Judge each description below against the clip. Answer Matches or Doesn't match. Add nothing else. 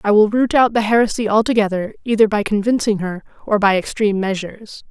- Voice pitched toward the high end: Matches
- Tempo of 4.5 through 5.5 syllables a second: Doesn't match